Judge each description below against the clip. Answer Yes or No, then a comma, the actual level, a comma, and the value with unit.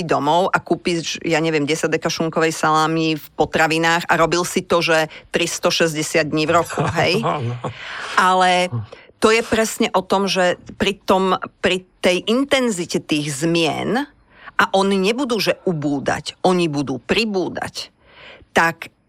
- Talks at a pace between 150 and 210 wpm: No, average, 140 wpm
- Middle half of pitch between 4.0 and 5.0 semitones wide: No, average, 3.3 semitones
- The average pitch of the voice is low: No, medium, 175 Hz